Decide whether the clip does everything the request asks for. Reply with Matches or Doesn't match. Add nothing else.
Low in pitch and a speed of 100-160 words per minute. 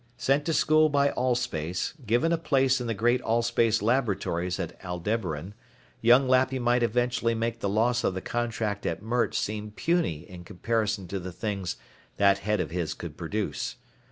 Doesn't match